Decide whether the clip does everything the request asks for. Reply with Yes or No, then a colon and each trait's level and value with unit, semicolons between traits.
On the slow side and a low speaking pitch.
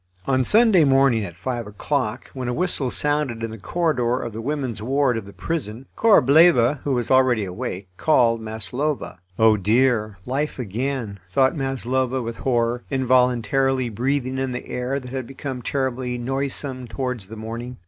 No: average, 160 wpm; low, 125 Hz